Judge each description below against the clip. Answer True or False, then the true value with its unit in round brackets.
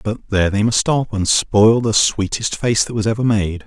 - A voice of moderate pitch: False (110 Hz)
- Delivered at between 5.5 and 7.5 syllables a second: False (4.9 syllables/s)